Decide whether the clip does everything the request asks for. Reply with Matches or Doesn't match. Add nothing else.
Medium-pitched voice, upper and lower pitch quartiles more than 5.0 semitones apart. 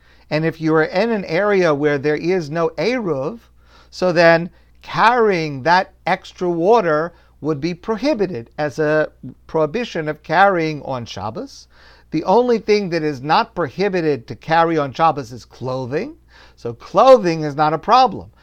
Doesn't match